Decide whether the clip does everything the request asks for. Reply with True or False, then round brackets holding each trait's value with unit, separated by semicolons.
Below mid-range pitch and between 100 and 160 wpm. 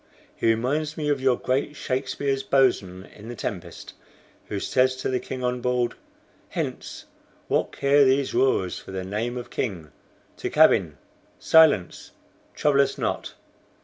True (130 Hz; 145 wpm)